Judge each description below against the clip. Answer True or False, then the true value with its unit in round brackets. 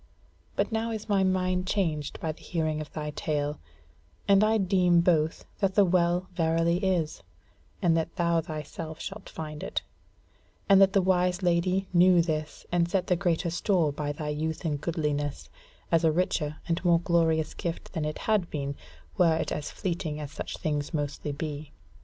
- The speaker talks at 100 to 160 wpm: False (175 wpm)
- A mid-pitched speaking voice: True (170 Hz)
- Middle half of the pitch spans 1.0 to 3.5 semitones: True (3.1 semitones)